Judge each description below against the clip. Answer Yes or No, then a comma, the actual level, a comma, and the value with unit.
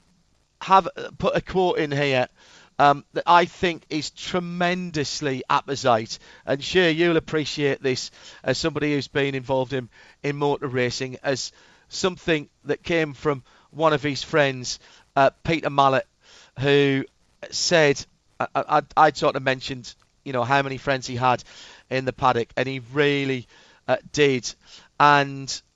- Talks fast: No, average, 140 wpm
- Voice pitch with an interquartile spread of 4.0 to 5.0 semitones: No, average, 3.0 semitones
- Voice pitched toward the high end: No, medium, 140 Hz